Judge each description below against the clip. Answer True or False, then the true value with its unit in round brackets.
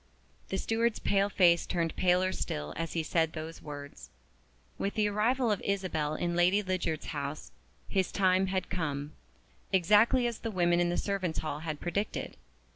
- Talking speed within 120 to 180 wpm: True (165 wpm)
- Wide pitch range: False (3.6 semitones)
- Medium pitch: True (180 Hz)